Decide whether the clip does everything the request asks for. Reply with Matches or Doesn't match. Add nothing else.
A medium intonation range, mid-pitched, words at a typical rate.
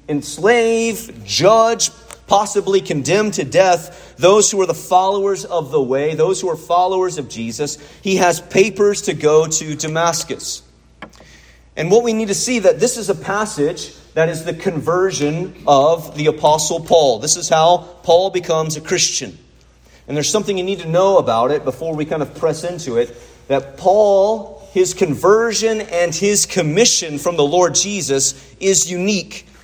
Matches